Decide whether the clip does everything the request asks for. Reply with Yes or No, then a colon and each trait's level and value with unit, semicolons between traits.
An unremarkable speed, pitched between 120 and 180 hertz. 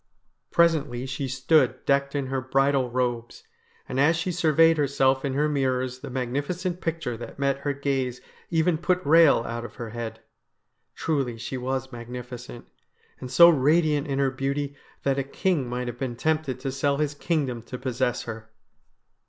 Yes: average, 170 wpm; low, 135 Hz